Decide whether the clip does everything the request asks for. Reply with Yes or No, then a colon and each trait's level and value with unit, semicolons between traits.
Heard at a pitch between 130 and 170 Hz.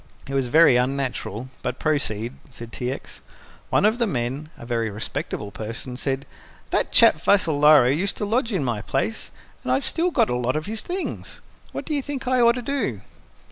Yes: low, 135 Hz